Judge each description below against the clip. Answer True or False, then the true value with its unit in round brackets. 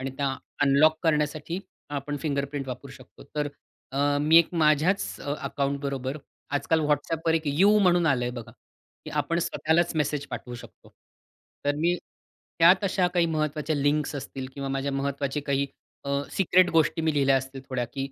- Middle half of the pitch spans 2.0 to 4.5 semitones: True (2.9 semitones)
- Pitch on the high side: False (145 Hz)